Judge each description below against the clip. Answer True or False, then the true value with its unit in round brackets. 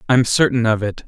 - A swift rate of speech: True (225 wpm)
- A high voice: False (120 Hz)